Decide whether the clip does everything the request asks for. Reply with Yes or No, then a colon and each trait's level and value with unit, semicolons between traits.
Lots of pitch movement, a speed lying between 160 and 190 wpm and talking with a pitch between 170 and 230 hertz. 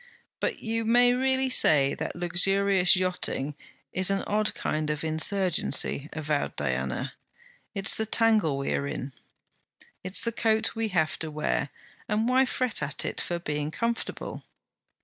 No: wide, 6.7 semitones; average, 150 wpm; medium, 185 Hz